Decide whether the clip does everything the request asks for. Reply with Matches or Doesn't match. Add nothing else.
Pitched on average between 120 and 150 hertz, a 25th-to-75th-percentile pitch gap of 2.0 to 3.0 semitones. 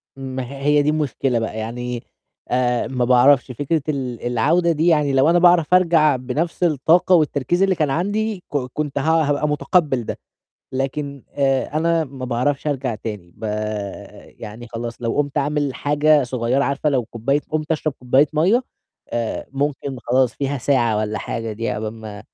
Doesn't match